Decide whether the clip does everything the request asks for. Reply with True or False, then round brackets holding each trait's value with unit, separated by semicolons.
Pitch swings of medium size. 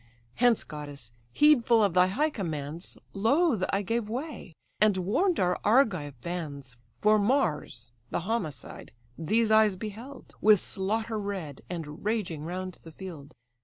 False (5.7 semitones)